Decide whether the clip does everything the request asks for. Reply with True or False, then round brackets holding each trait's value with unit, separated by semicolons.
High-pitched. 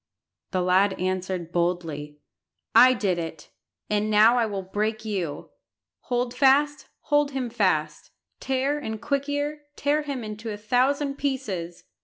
True (215 Hz)